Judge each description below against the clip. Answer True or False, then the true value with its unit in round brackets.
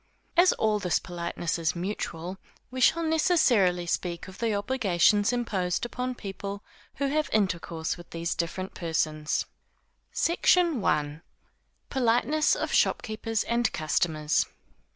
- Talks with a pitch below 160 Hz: False (200 Hz)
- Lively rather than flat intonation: True (6.2 semitones)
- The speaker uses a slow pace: True (120 wpm)